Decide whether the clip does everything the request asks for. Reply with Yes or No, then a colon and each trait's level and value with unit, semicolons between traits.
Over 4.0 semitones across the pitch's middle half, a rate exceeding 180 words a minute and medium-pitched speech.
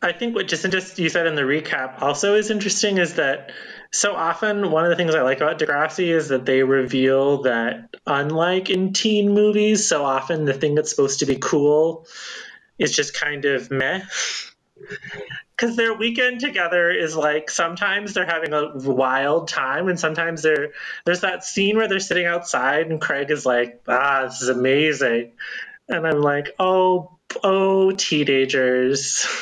No: wide, 5.4 semitones; average, 170 wpm; medium, 160 Hz